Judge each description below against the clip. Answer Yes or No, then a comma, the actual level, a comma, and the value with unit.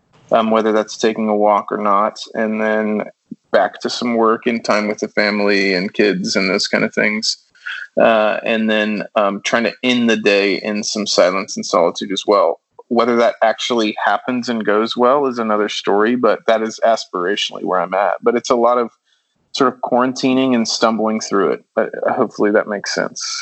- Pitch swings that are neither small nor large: No, narrow, 2.1 semitones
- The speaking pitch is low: Yes, low, 110 Hz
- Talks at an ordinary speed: Yes, average, 195 wpm